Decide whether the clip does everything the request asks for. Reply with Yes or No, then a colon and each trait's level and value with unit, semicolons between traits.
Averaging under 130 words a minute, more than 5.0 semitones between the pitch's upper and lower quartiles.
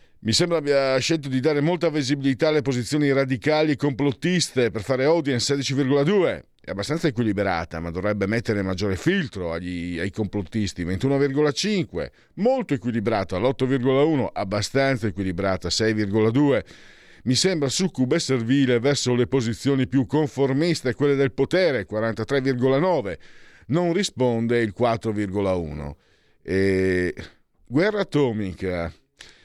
Yes: slow, 115 wpm; wide, 5.6 semitones